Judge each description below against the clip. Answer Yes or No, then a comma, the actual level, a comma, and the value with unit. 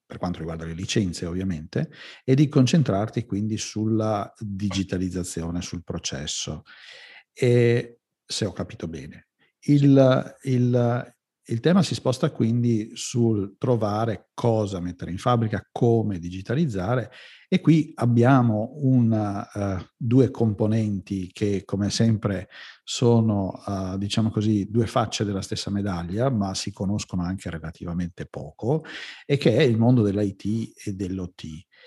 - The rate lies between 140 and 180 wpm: No, average, 125 wpm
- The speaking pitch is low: Yes, low, 110 Hz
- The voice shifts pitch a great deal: No, average, 3.9 semitones